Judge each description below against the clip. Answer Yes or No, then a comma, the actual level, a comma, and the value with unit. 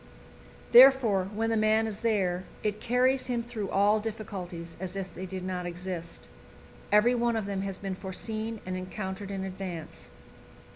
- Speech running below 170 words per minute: Yes, average, 160 wpm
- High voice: Yes, high, 200 Hz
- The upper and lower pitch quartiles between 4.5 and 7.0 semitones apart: No, average, 3.1 semitones